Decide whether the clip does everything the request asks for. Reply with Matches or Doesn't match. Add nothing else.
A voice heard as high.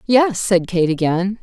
Matches